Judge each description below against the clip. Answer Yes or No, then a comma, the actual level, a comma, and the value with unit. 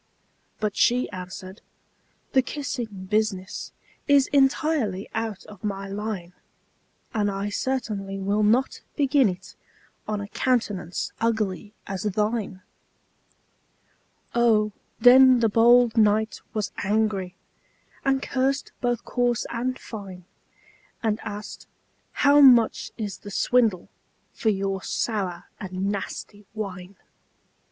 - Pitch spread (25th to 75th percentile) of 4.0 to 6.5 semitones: No, average, 3.6 semitones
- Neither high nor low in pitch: No, high, 215 Hz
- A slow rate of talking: Yes, slow, 110 wpm